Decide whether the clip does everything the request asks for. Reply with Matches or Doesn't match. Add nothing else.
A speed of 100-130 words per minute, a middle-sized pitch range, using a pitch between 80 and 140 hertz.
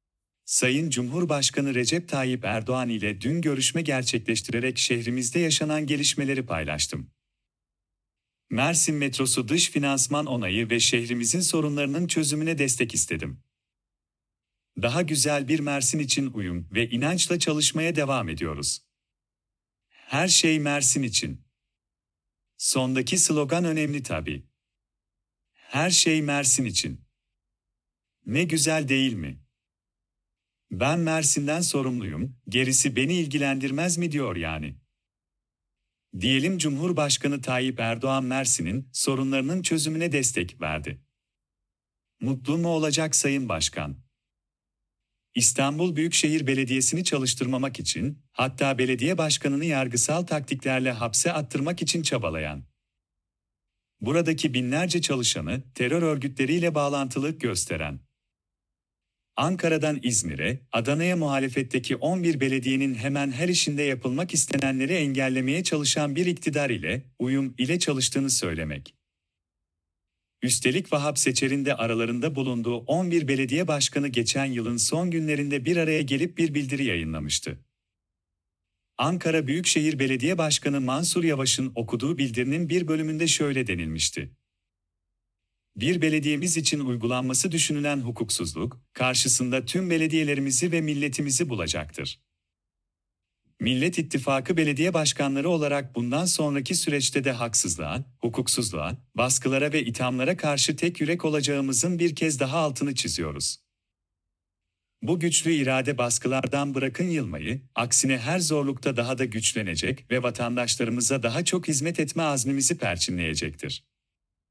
Matches